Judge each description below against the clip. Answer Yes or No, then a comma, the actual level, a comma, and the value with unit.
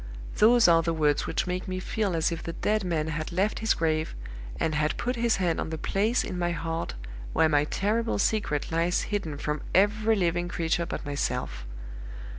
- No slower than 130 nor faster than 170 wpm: No, average, 195 wpm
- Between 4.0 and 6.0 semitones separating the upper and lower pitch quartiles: Yes, average, 4.5 semitones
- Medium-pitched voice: Yes, medium, 170 Hz